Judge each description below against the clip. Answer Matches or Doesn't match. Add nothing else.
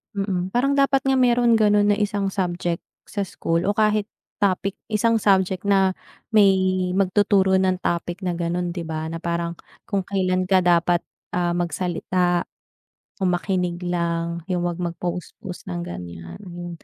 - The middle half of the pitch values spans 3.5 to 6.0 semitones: Doesn't match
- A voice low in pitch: Doesn't match